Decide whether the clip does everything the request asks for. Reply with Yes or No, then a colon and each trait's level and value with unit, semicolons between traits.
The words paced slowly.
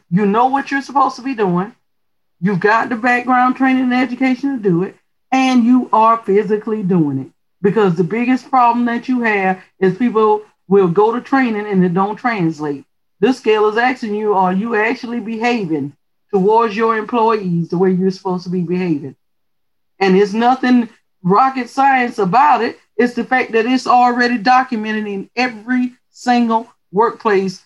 No: average, 170 wpm